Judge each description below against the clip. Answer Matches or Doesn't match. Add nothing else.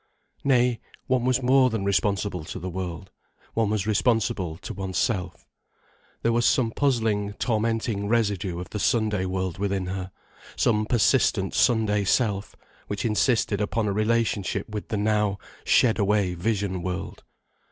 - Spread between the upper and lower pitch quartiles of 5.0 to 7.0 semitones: Doesn't match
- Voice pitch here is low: Matches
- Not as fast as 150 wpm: Matches